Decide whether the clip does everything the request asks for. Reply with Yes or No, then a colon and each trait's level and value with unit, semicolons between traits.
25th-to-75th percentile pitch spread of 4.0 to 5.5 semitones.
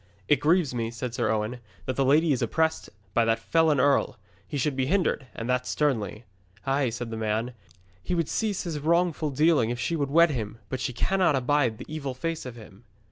Yes: average, 4.9 semitones